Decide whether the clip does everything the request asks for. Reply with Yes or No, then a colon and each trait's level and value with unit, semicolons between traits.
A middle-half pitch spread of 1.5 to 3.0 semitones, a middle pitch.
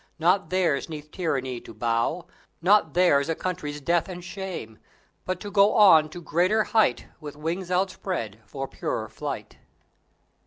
No: average, 4.1 semitones; medium, 170 Hz